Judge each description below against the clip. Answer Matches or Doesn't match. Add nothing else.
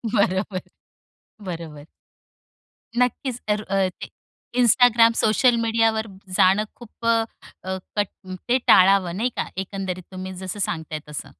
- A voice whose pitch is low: Doesn't match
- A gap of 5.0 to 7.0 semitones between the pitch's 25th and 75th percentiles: Doesn't match